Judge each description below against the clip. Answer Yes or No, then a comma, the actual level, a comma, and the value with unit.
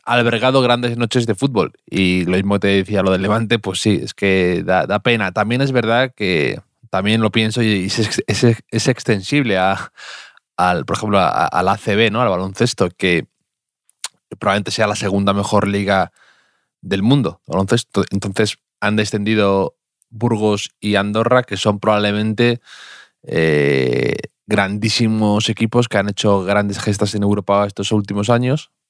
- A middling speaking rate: Yes, average, 145 wpm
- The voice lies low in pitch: Yes, low, 105 Hz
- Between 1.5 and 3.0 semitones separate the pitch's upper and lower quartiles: Yes, narrow, 2.6 semitones